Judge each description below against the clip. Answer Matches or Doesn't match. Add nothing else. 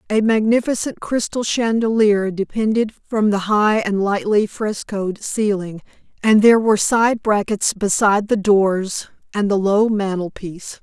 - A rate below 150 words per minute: Matches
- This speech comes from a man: Doesn't match